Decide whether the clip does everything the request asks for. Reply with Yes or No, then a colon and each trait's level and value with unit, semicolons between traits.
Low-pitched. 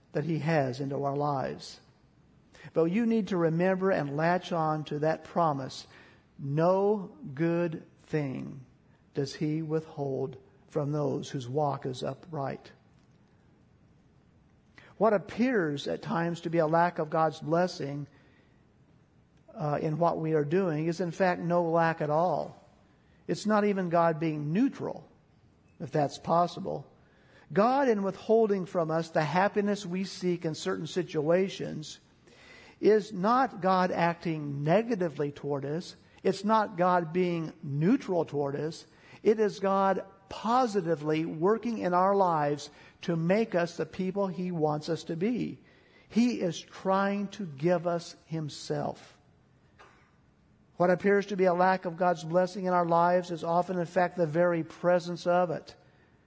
No: medium, 170 Hz